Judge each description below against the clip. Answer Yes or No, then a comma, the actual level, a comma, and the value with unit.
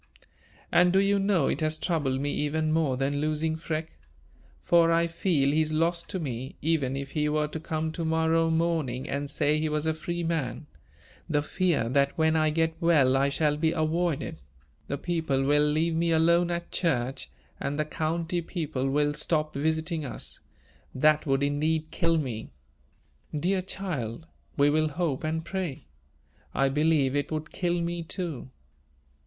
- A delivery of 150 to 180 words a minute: Yes, average, 170 wpm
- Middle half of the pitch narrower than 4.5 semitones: Yes, narrow, 2.6 semitones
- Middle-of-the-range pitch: Yes, medium, 155 Hz